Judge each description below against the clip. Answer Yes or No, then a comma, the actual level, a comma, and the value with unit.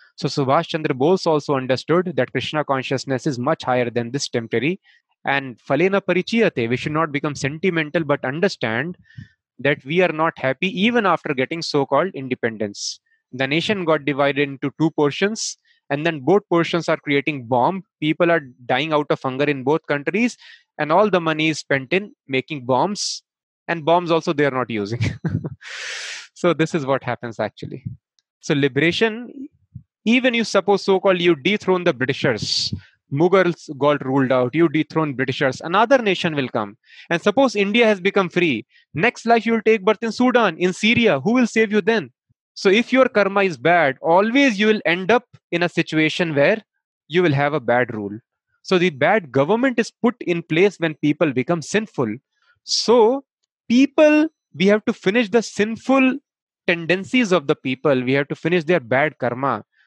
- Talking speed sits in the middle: Yes, average, 175 wpm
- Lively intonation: Yes, wide, 6.5 semitones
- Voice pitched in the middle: Yes, medium, 170 Hz